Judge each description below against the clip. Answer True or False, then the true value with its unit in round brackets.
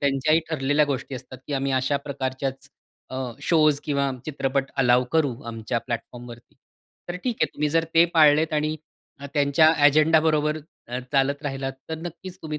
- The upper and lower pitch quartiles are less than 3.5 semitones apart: True (2.6 semitones)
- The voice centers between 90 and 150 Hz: True (140 Hz)